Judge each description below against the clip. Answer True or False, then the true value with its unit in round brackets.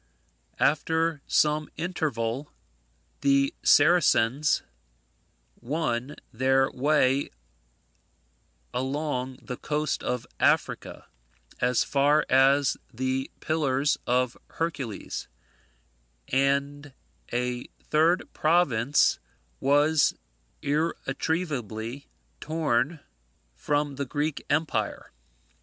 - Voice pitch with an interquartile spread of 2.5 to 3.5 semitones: True (3.0 semitones)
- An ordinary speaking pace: False (75 wpm)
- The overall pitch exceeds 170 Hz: False (140 Hz)